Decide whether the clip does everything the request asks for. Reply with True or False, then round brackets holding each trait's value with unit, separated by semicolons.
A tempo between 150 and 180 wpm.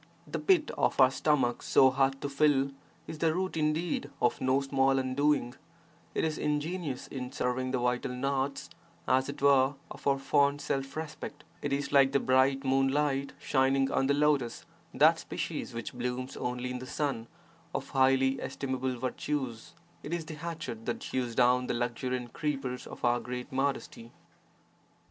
True (165 wpm)